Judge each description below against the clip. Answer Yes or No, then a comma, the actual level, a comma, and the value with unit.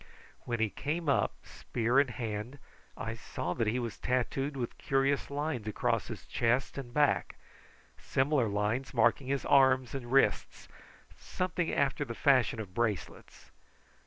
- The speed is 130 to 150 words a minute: Yes, average, 145 wpm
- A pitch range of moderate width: Yes, average, 3.3 semitones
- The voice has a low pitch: Yes, low, 125 Hz